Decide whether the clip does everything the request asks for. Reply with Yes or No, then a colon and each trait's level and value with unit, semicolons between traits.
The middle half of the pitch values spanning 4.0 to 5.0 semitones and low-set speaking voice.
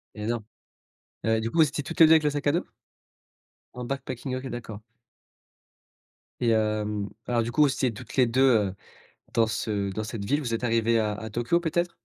Yes: average, 4.3 semitones; low, 120 Hz